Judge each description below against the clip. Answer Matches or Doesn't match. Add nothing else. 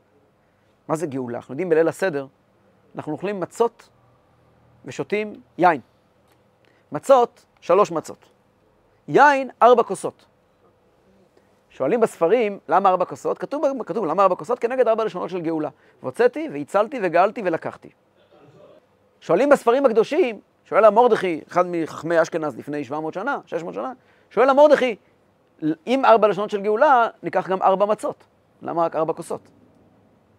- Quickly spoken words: Doesn't match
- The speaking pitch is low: Doesn't match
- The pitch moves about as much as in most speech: Doesn't match